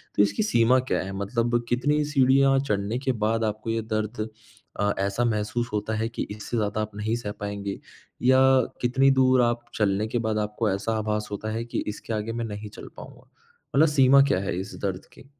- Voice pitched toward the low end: Yes, low, 110 Hz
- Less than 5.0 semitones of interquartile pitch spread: Yes, average, 2.9 semitones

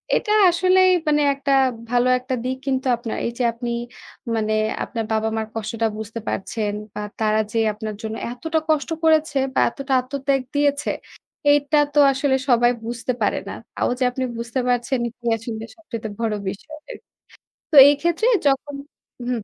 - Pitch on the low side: No, very high, 250 Hz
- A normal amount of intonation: Yes, average, 4.3 semitones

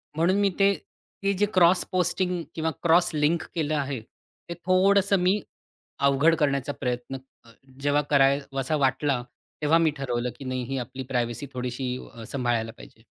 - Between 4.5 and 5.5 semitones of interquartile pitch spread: Yes, average, 5.0 semitones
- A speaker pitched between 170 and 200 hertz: No, medium, 145 Hz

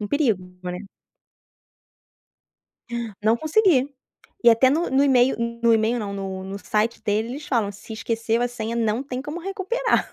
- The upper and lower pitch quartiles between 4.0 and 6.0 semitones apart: Yes, average, 4.3 semitones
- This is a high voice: Yes, high, 235 Hz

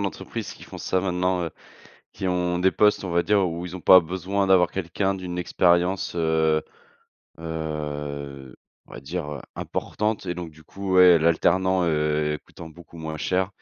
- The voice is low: Yes, very low, 90 Hz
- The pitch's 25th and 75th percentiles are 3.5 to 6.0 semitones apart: No, average, 2.8 semitones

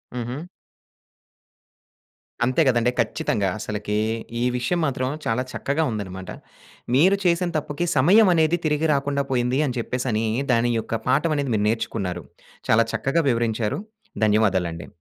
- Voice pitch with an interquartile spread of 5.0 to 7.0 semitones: Yes, average, 5.3 semitones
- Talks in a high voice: No, low, 125 Hz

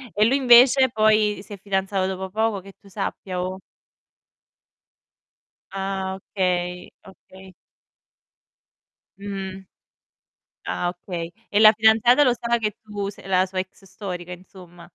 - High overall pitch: Yes, high, 195 Hz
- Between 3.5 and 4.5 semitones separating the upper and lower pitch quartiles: No, narrow, 2.5 semitones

